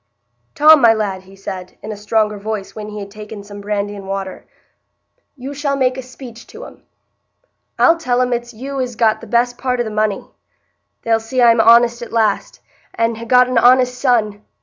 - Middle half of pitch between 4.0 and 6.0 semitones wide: No, average, 3.0 semitones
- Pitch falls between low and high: No, high, 230 Hz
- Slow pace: No, average, 200 wpm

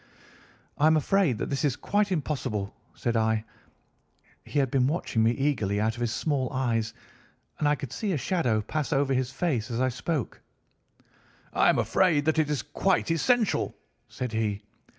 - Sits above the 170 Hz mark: No, low, 135 Hz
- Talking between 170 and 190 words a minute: Yes, average, 175 wpm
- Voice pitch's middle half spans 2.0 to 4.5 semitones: No, wide, 5.4 semitones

